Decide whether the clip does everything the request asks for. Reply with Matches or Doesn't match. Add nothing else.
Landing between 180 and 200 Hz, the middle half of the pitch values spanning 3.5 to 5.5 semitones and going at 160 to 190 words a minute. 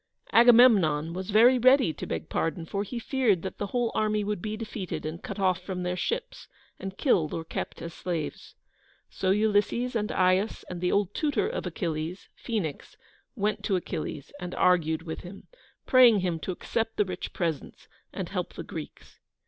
Matches